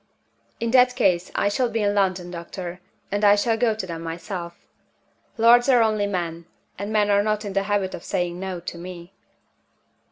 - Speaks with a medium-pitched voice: No, high, 200 Hz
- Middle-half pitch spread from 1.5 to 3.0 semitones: No, average, 3.4 semitones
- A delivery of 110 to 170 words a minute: No, average, 190 wpm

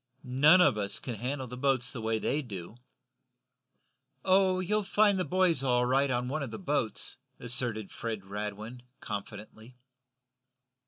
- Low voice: Yes, low, 125 Hz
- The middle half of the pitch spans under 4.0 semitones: No, average, 5.2 semitones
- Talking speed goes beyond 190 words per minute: No, average, 150 wpm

